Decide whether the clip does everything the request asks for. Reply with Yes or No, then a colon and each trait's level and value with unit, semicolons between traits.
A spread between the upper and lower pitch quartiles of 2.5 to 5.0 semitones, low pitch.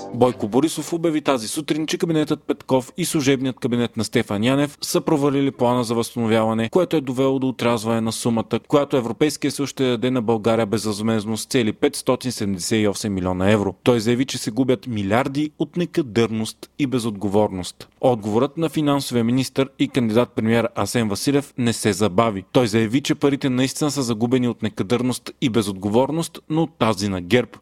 Yes: average, 3.9 semitones; low, 125 Hz